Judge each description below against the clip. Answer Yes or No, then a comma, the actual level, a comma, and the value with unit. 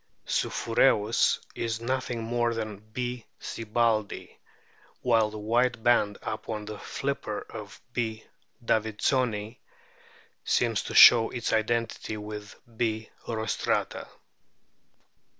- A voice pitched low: Yes, low, 115 Hz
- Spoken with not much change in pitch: Yes, narrow, 1.7 semitones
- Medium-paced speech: No, slow, 95 wpm